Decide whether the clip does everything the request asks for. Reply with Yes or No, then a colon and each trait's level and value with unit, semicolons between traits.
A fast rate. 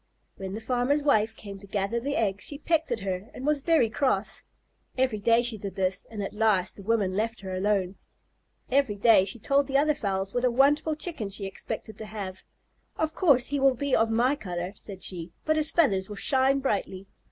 Yes: fast, 210 wpm